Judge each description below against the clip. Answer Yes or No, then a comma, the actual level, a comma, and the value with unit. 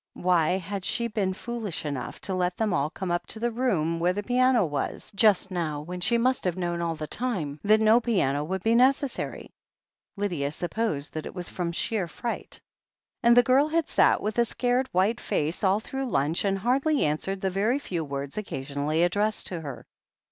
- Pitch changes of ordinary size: No, wide, 6.0 semitones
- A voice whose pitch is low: No, high, 190 Hz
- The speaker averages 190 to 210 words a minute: Yes, average, 200 wpm